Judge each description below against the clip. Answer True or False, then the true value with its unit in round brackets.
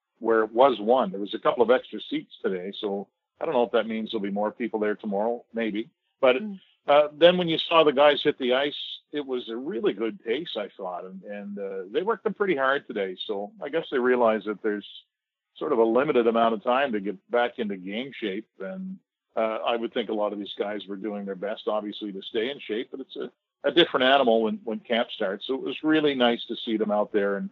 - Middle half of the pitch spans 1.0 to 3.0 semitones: False (5.1 semitones)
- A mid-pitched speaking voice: False (115 Hz)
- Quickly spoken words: True (250 wpm)